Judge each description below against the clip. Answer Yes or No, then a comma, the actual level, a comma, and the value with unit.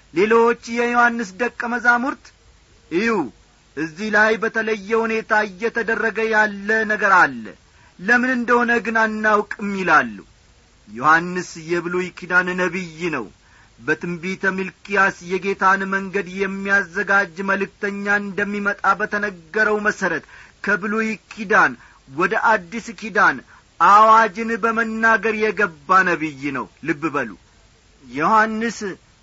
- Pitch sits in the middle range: No, high, 205 Hz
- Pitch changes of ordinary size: Yes, average, 3.6 semitones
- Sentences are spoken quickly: No, average, 90 wpm